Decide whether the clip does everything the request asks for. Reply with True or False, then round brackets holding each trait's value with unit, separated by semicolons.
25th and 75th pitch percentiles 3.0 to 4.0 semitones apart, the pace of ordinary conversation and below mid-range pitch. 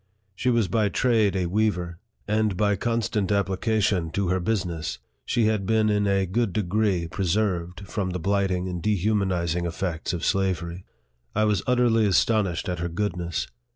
True (3.4 semitones; 160 wpm; 100 Hz)